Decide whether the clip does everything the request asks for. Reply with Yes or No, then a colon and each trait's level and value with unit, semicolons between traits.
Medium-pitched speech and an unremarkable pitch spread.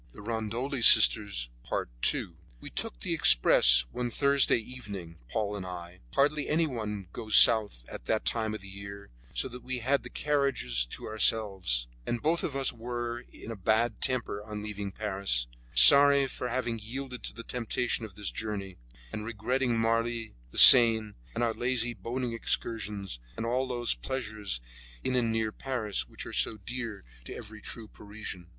No: low, 110 Hz; average, 3.5 semitones